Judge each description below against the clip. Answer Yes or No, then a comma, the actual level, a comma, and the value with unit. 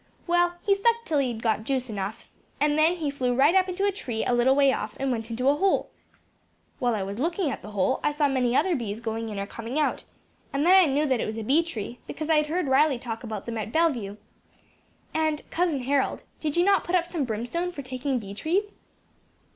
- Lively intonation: Yes, wide, 6.2 semitones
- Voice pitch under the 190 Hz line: No, very high, 275 Hz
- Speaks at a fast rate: Yes, fast, 235 wpm